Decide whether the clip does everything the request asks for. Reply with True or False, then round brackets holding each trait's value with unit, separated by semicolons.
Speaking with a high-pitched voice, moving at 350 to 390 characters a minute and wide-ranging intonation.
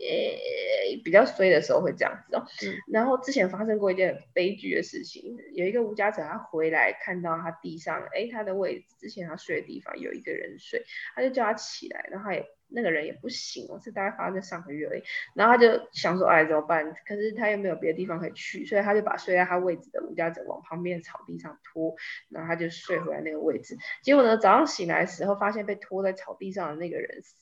True (200 Hz; 360 characters per minute; 7.5 semitones)